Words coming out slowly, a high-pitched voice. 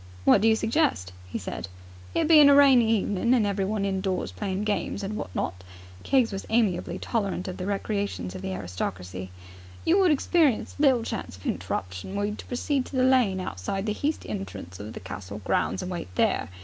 No: average, 200 wpm; high, 200 Hz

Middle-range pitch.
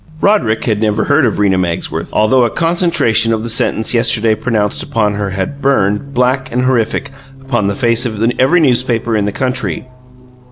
No: low, 115 Hz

